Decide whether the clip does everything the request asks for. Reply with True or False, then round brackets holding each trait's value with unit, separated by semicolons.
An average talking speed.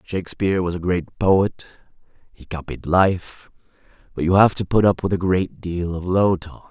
True (190 wpm)